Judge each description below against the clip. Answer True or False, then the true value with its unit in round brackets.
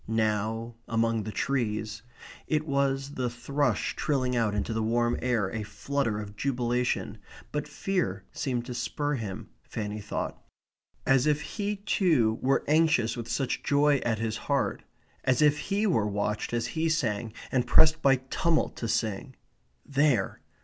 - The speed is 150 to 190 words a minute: True (155 wpm)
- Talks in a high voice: False (120 Hz)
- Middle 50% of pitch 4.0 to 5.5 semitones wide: True (4.5 semitones)